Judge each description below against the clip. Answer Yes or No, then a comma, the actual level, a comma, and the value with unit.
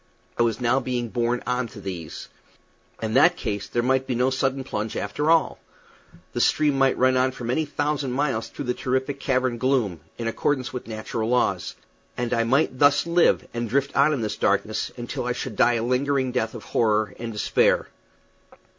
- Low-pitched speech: Yes, low, 125 Hz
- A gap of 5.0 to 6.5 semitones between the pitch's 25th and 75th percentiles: No, average, 2.7 semitones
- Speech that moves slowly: No, average, 190 wpm